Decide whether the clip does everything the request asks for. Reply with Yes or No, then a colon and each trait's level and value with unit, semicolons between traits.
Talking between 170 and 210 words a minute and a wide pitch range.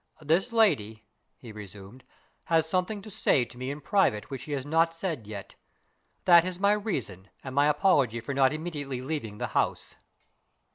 Yes: average, 175 wpm; wide, 6.7 semitones